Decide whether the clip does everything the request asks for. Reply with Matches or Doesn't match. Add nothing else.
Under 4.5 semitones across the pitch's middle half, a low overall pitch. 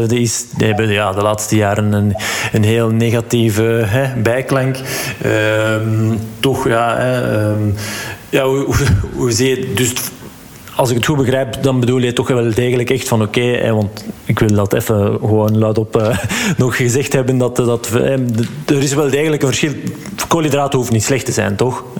Matches